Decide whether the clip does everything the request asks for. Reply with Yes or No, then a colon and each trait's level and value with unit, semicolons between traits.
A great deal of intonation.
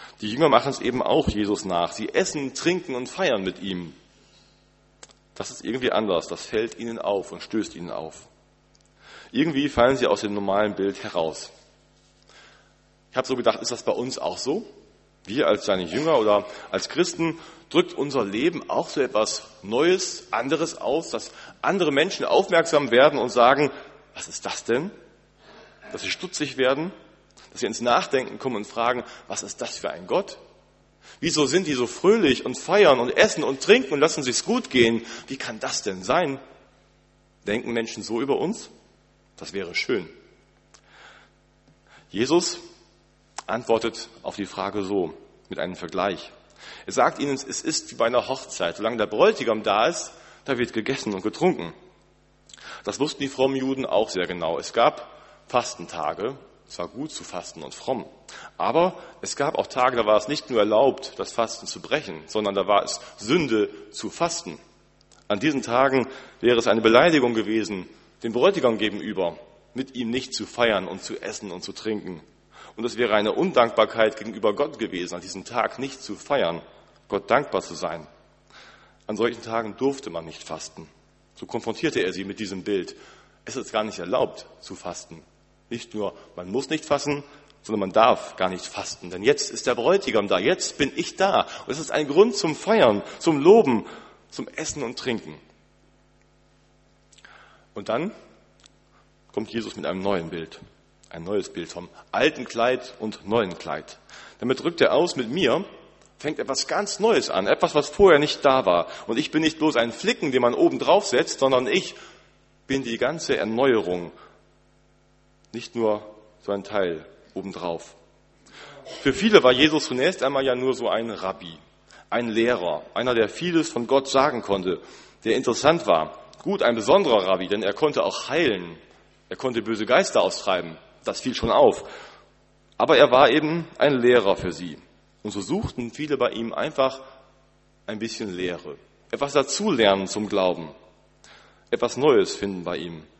Yes: wide, 5.7 semitones